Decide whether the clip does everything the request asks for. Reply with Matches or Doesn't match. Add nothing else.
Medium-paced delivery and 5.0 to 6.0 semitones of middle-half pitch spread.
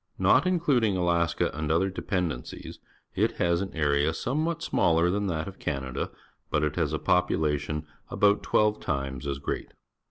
Matches